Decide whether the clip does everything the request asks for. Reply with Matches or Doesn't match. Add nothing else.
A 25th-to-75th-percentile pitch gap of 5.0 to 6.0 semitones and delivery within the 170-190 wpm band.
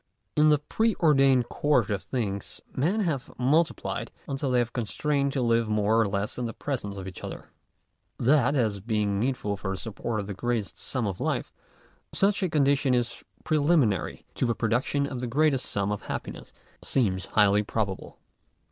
Matches